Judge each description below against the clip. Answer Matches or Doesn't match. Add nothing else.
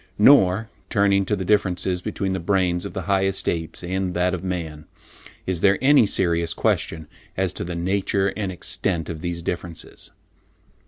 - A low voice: Matches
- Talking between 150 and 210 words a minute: Matches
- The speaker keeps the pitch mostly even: Matches